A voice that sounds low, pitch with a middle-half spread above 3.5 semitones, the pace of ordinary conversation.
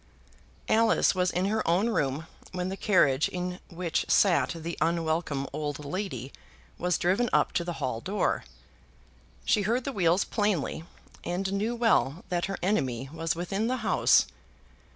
No: medium, 180 Hz; average, 4.1 semitones; average, 150 wpm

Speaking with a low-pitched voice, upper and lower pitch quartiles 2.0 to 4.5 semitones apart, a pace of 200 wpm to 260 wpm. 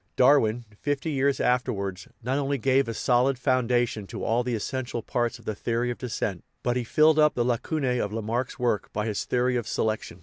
Yes: low, 125 Hz; narrow, 2.6 semitones; fast, 205 wpm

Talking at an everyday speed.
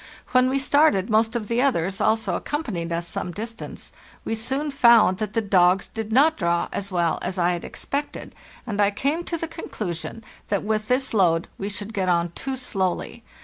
Yes: average, 190 wpm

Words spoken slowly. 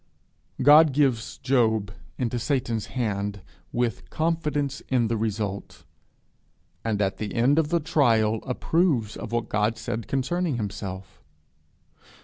Yes: slow, 125 wpm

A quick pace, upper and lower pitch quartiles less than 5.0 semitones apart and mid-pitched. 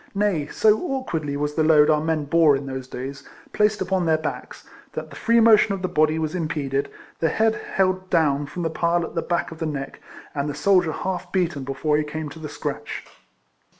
Yes: fast, 215 wpm; average, 3.9 semitones; medium, 160 Hz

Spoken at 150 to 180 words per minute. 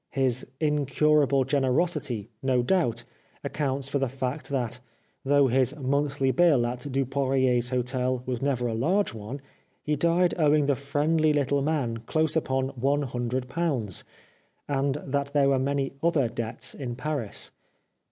No: average, 140 wpm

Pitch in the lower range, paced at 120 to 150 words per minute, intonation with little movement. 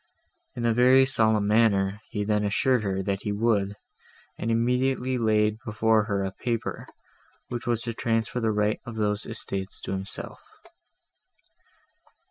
Yes: low, 110 Hz; average, 145 wpm; narrow, 2.2 semitones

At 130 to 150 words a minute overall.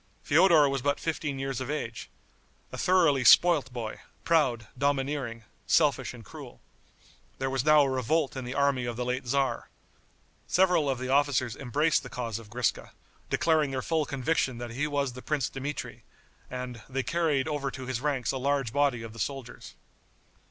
No: average, 175 wpm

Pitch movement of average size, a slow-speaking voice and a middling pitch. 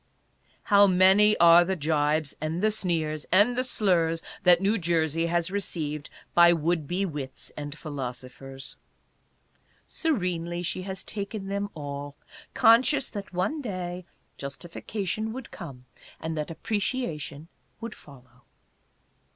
Yes: average, 4.8 semitones; slow, 125 wpm; medium, 175 Hz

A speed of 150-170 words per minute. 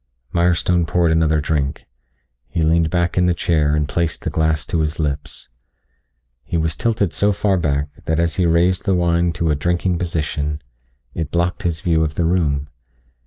No: average, 180 wpm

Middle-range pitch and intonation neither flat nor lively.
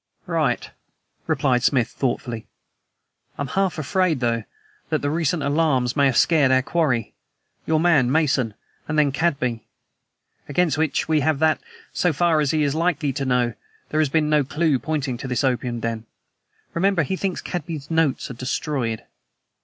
Yes: medium, 145 Hz; average, 3.9 semitones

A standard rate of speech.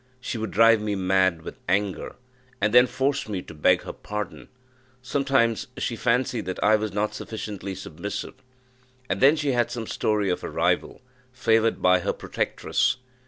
Yes: average, 165 wpm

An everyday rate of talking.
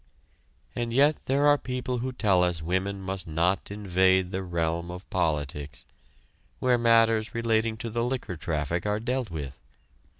Yes: average, 155 wpm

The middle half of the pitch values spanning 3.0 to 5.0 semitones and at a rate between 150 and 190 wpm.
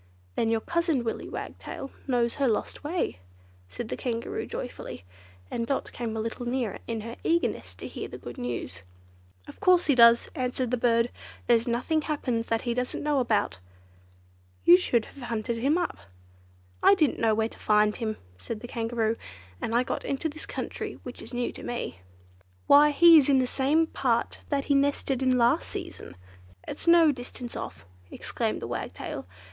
Yes: average, 3.5 semitones; average, 180 wpm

